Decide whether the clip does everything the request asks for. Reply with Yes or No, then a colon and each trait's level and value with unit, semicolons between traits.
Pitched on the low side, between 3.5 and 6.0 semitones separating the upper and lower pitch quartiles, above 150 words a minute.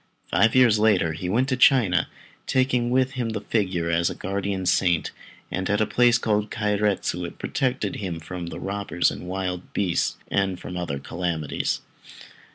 Yes: low, 100 Hz; average, 4.0 semitones; average, 165 wpm